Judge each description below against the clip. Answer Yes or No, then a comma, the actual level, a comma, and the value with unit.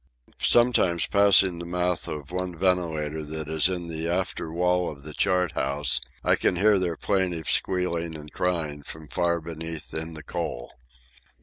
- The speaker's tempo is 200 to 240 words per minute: No, average, 165 wpm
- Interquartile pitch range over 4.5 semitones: No, narrow, 2.5 semitones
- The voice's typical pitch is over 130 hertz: No, very low, 85 Hz